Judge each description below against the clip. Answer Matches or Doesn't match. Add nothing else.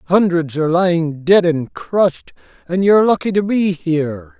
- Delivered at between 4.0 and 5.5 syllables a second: Matches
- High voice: Doesn't match